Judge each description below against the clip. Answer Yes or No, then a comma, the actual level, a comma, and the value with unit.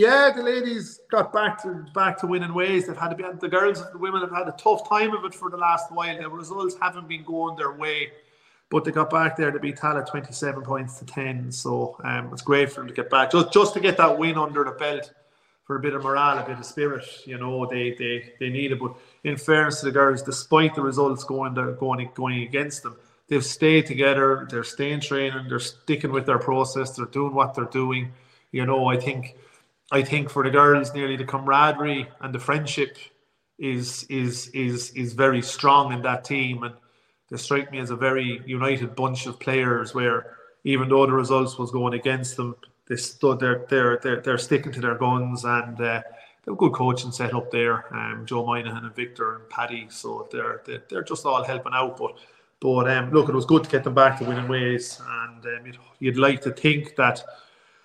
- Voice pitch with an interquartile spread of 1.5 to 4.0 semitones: Yes, average, 3.4 semitones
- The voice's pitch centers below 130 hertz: No, low, 135 Hz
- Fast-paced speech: Yes, fast, 225 wpm